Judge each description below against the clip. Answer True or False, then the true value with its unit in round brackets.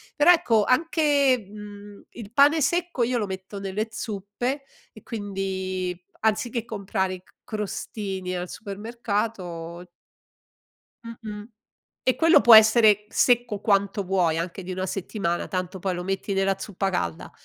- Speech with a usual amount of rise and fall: True (3.5 semitones)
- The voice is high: True (205 Hz)